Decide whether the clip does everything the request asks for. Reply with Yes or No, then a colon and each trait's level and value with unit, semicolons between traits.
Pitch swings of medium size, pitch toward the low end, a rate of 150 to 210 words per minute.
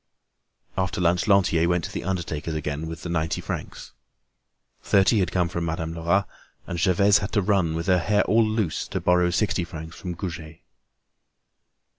Yes: average, 3.0 semitones; very low, 90 Hz; average, 165 wpm